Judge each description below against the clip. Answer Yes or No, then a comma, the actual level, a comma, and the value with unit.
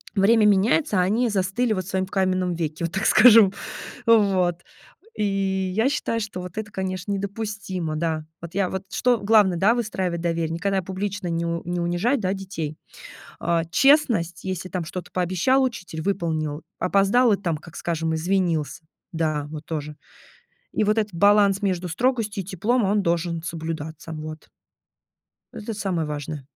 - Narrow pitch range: No, average, 3.6 semitones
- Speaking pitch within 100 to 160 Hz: No, medium, 185 Hz